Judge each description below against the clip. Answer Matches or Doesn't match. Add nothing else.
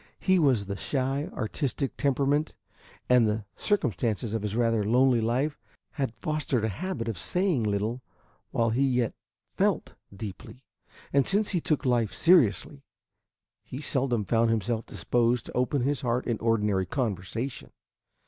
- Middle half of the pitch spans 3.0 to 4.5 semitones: Matches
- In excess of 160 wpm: Doesn't match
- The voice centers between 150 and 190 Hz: Doesn't match